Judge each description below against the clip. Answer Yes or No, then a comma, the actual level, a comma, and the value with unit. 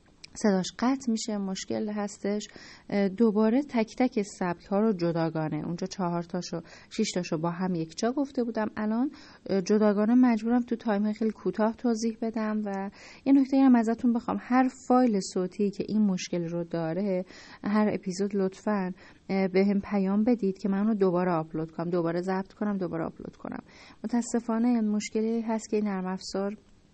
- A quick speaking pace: Yes, fast, 160 wpm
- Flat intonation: No, average, 3.4 semitones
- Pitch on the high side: Yes, high, 205 Hz